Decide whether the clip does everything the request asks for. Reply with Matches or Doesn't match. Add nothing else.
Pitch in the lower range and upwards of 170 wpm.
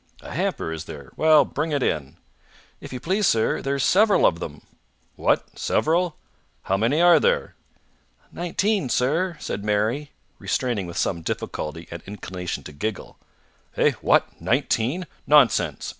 Doesn't match